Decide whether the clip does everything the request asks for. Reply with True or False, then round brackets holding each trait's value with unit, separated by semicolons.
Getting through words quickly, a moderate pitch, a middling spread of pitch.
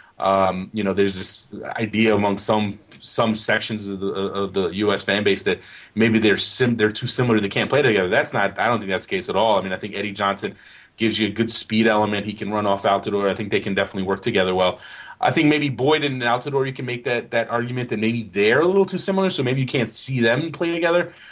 False (255 wpm; 110 Hz; 4.0 semitones)